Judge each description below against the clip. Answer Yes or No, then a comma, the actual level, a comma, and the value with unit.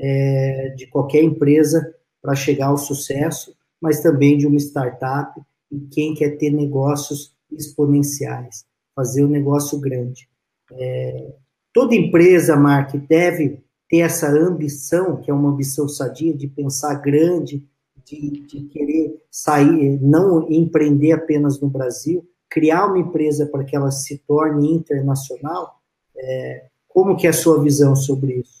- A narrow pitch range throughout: Yes, narrow, 2.0 semitones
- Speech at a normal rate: Yes, average, 140 wpm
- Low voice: No, medium, 145 Hz